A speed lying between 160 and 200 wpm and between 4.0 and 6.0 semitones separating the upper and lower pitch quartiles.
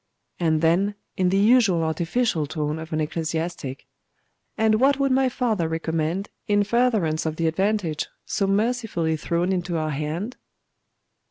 No: average, 145 wpm; average, 5.1 semitones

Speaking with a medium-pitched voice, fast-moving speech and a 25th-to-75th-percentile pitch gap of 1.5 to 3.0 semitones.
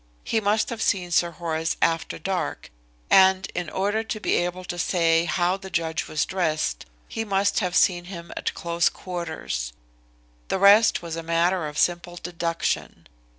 No: medium, 175 Hz; average, 165 wpm; narrow, 2.4 semitones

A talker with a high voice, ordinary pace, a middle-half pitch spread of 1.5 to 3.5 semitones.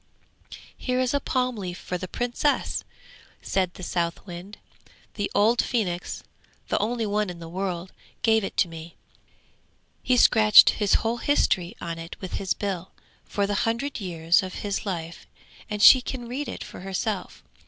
No: high, 200 Hz; average, 165 wpm; average, 4.5 semitones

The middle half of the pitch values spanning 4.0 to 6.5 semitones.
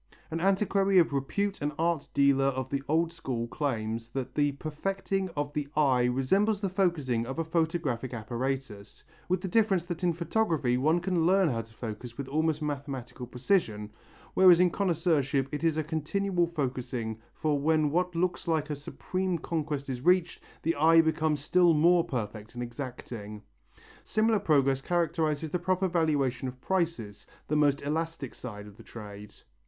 Yes: average, 5.0 semitones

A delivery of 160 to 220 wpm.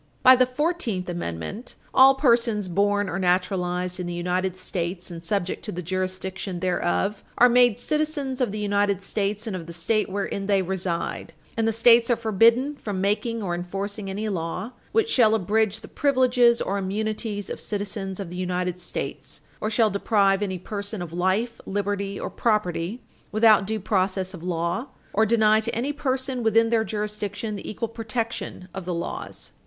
Yes: average, 175 wpm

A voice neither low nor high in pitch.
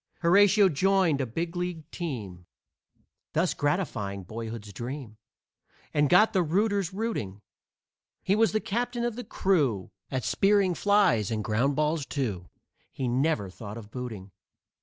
Yes: medium, 150 Hz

